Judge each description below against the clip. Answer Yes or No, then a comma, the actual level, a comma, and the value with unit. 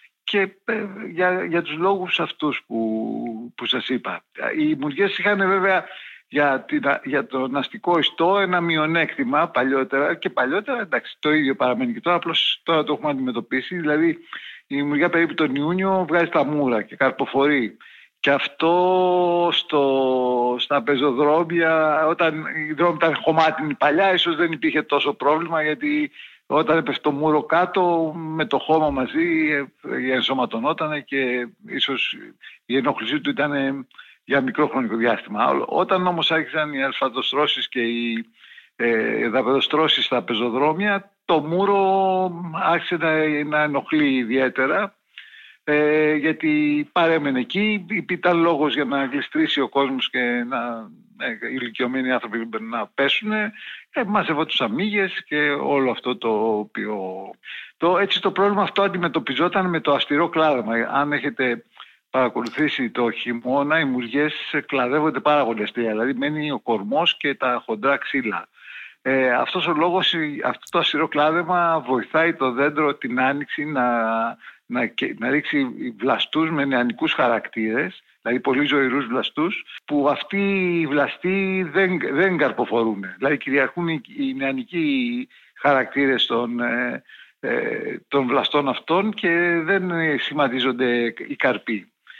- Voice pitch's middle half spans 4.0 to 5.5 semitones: Yes, average, 4.8 semitones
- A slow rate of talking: No, average, 135 wpm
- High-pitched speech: No, medium, 150 Hz